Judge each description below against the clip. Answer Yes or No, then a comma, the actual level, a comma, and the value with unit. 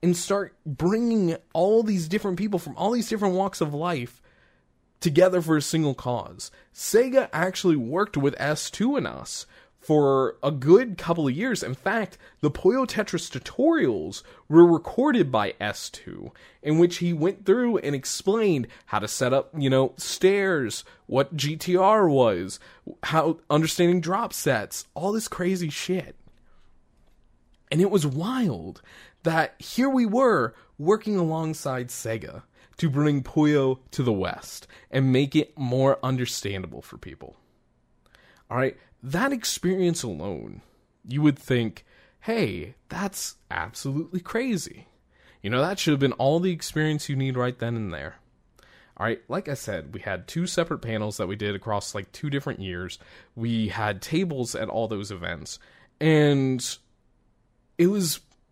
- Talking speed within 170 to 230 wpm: No, average, 150 wpm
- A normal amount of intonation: No, wide, 6.6 semitones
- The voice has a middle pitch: Yes, medium, 150 Hz